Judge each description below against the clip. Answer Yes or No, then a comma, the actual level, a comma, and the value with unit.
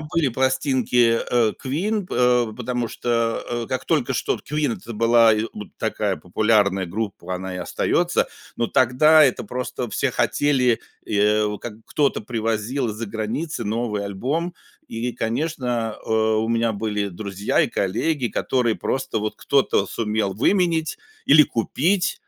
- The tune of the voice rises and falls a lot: No, average, 3.7 semitones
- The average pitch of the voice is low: Yes, low, 115 Hz